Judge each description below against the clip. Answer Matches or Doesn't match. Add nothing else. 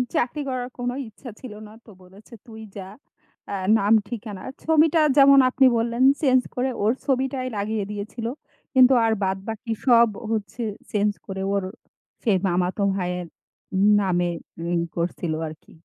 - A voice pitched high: Matches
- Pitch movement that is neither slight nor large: Matches